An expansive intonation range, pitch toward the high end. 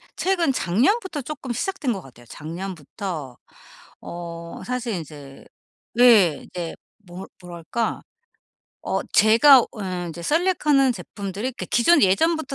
Yes: wide, 7.9 semitones; high, 205 Hz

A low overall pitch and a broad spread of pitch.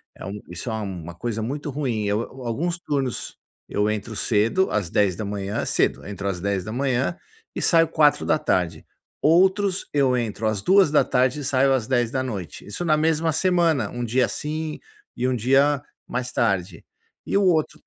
Yes: low, 125 Hz; wide, 6.5 semitones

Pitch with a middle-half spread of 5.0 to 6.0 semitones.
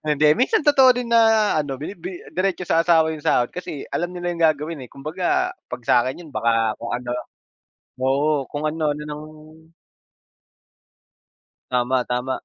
Yes: wide, 5.4 semitones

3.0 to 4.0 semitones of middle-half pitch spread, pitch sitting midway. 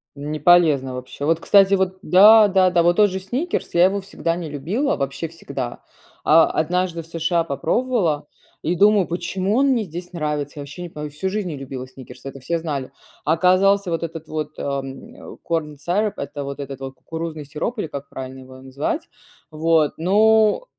No: average, 4.8 semitones; medium, 165 Hz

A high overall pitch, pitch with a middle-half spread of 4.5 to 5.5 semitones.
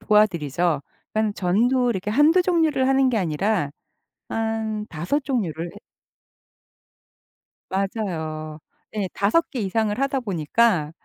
No: high, 210 Hz; wide, 5.9 semitones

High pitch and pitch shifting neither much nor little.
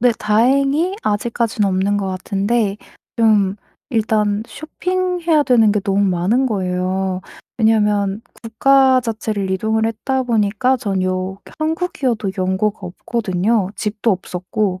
Yes: high, 215 Hz; average, 3.7 semitones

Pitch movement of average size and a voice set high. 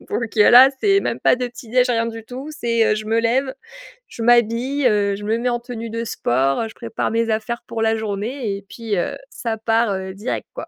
No: narrow, 2.0 semitones; high, 230 Hz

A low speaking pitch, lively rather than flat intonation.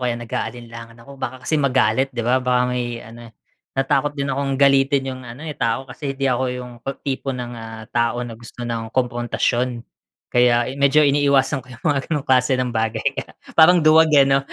No: low, 130 Hz; narrow, 2.5 semitones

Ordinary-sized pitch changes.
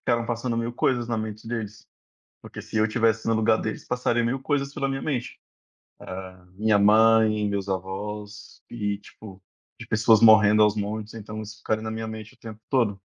No: narrow, 1.7 semitones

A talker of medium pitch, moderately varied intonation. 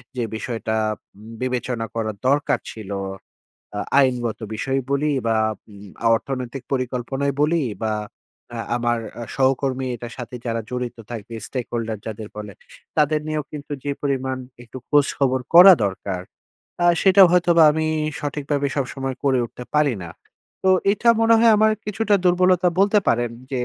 No: low, 130 Hz; average, 4.2 semitones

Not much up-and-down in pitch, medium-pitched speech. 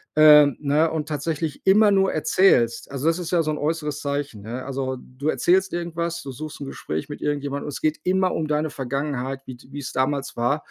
No: average, 3.0 semitones; medium, 150 Hz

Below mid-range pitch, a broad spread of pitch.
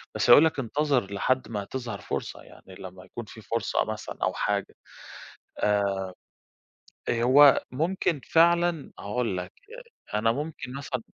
Yes: low, 125 Hz; wide, 5.8 semitones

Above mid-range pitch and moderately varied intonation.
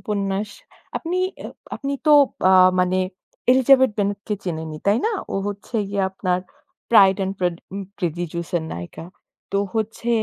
Yes: high, 200 Hz; average, 3.5 semitones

